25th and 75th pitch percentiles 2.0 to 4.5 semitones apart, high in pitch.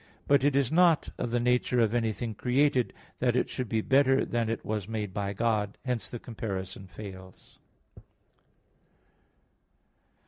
No: average, 3.2 semitones; low, 115 Hz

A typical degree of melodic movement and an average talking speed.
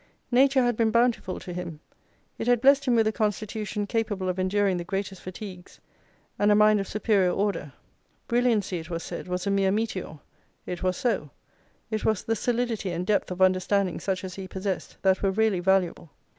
Yes: average, 3.0 semitones; average, 190 wpm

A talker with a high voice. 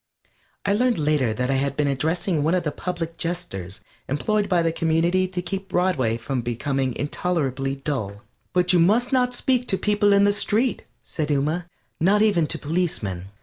No: medium, 165 Hz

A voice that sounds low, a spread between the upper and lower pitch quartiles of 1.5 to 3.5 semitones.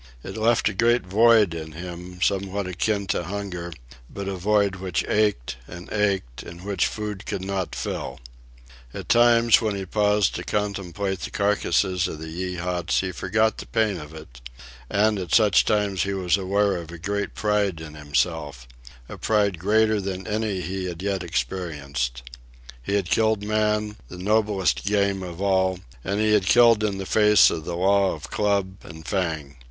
Yes: very low, 95 Hz; average, 3.1 semitones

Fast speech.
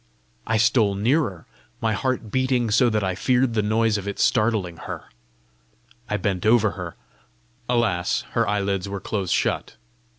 No: average, 155 wpm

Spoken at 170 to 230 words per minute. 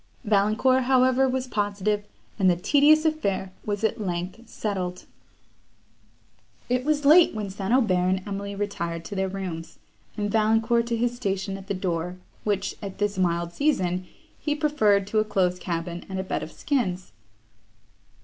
No: average, 160 wpm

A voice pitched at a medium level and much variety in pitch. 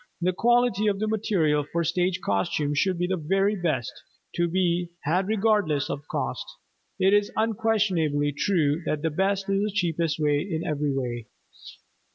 No: medium, 175 Hz; average, 5.0 semitones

